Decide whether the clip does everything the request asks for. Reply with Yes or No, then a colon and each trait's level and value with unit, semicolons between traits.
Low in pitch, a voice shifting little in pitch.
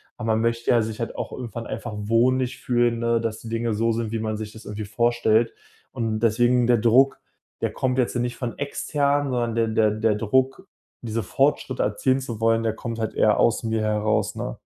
Yes: low, 115 Hz; narrow, 1.8 semitones